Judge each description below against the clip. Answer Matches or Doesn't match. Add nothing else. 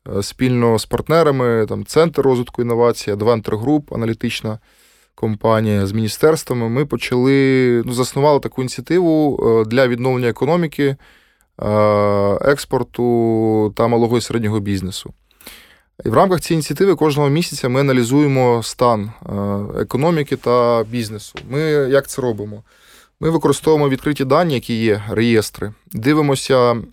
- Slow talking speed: Doesn't match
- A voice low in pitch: Matches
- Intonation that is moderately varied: Matches